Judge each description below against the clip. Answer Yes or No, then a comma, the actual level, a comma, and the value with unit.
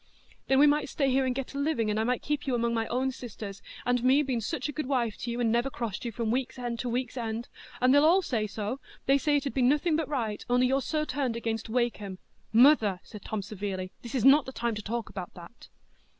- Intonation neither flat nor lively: Yes, average, 3.4 semitones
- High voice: Yes, high, 245 Hz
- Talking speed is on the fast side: Yes, fast, 240 wpm